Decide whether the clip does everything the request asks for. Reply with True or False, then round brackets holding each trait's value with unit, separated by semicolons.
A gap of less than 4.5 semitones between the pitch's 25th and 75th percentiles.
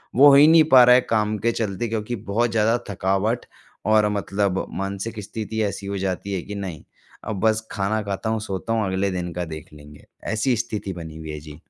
True (2.9 semitones)